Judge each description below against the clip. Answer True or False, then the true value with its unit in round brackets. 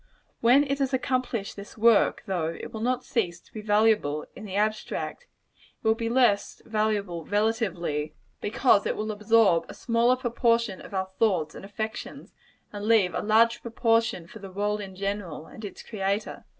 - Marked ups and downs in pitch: False (2.8 semitones)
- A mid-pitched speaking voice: False (215 Hz)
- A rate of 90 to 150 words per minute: False (175 wpm)